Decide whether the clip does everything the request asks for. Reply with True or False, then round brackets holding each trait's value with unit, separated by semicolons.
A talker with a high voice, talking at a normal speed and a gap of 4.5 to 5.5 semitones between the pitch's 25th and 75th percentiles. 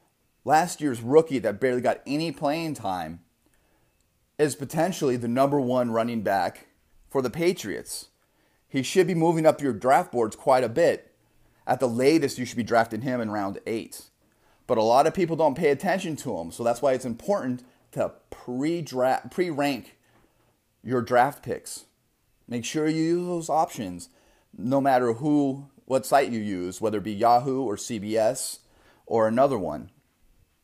False (130 Hz; 165 wpm; 4.8 semitones)